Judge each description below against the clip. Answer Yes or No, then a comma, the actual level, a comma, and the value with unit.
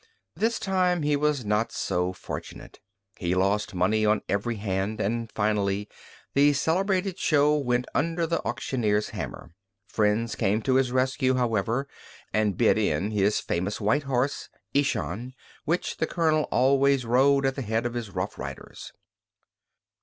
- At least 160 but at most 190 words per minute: No, average, 145 wpm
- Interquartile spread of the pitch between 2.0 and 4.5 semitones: No, wide, 5.4 semitones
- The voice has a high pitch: No, low, 120 Hz